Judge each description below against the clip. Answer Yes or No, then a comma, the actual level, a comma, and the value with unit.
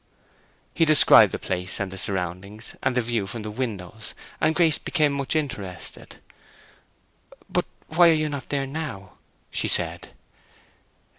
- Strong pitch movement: Yes, wide, 7.5 semitones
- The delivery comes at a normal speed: Yes, average, 145 wpm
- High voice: No, low, 120 Hz